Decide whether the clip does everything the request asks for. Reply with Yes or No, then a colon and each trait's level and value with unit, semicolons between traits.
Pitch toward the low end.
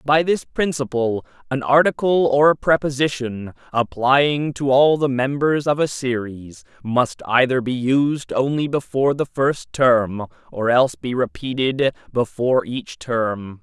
Yes: low, 130 Hz